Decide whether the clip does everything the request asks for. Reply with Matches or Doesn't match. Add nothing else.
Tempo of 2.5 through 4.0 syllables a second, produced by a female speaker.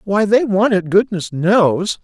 Doesn't match